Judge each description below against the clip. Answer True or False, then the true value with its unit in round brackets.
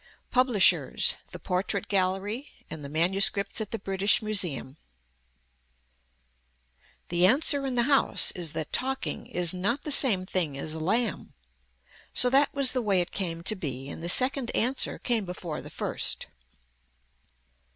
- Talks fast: False (150 wpm)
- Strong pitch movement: True (6.0 semitones)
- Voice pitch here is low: False (195 Hz)